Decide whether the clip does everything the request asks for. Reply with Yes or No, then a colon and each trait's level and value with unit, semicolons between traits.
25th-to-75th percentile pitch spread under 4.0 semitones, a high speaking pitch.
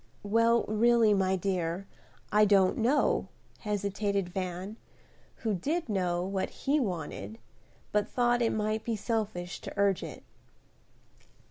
Yes: average, 3.1 semitones; high, 205 Hz